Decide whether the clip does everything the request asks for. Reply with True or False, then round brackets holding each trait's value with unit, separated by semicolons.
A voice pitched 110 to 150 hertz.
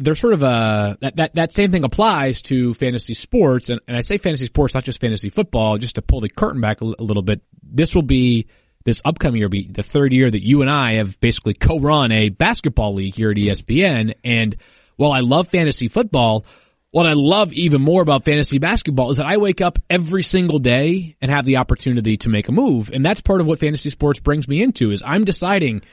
True (135 Hz)